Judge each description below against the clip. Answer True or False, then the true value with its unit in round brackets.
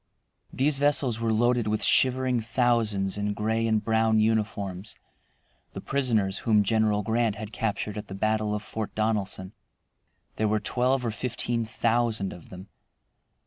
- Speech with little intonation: True (2.2 semitones)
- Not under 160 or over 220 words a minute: False (145 wpm)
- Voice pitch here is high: False (110 Hz)